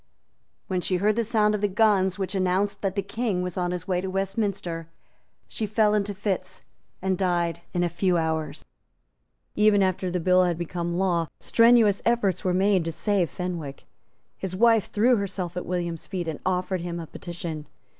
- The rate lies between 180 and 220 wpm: Yes, average, 185 wpm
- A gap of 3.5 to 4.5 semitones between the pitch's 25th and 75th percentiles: No, narrow, 2.6 semitones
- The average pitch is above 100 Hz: Yes, medium, 185 Hz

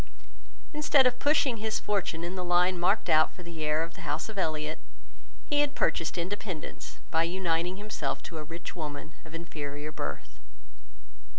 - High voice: No, medium, 170 Hz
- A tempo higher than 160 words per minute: Yes, average, 170 wpm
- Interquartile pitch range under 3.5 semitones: No, average, 4.7 semitones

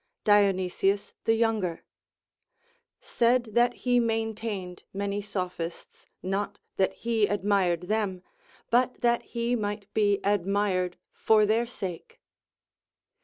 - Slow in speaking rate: Yes, slow, 105 wpm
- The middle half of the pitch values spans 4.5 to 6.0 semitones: No, average, 2.9 semitones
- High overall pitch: Yes, high, 205 Hz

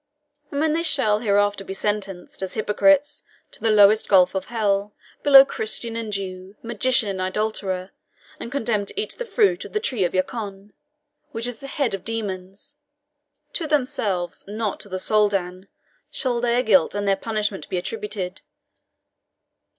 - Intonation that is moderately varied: Yes, average, 3.7 semitones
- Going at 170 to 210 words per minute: No, average, 160 wpm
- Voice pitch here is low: No, high, 210 Hz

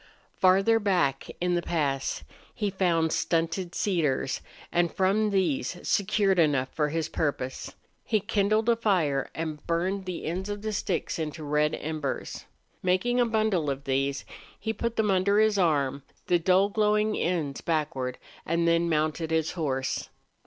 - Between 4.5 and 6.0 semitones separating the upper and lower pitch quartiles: Yes, average, 4.8 semitones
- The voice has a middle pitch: Yes, medium, 170 Hz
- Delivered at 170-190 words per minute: No, average, 155 wpm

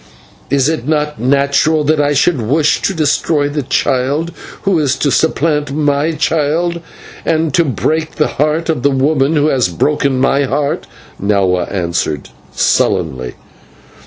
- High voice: No, medium, 145 Hz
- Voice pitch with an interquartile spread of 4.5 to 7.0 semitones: No, average, 2.9 semitones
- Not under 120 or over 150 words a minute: Yes, average, 145 wpm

